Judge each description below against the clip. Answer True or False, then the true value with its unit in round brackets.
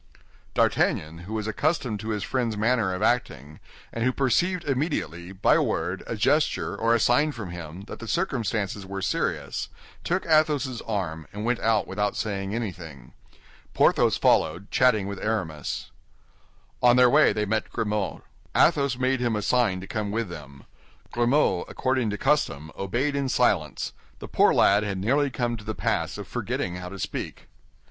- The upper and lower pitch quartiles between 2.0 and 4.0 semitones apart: False (4.9 semitones)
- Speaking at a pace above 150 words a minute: True (170 wpm)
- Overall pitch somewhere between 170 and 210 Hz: False (110 Hz)